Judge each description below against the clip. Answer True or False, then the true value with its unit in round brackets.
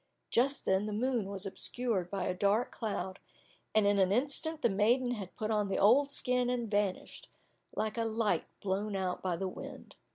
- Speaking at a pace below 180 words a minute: False (190 wpm)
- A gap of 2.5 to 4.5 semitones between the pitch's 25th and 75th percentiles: True (3.9 semitones)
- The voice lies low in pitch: False (210 Hz)